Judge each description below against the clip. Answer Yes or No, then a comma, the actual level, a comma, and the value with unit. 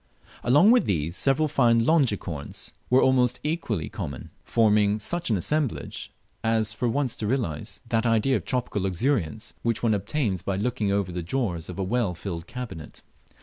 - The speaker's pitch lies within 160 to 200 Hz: No, low, 115 Hz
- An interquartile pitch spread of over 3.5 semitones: Yes, average, 5.0 semitones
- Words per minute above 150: Yes, average, 165 wpm